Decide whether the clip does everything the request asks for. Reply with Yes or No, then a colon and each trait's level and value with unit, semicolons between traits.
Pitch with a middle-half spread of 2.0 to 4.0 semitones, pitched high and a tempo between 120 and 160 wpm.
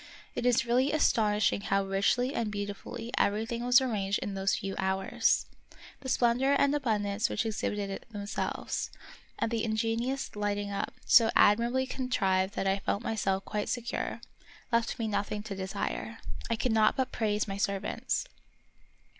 Yes: average, 2.9 semitones; high, 215 Hz; average, 155 wpm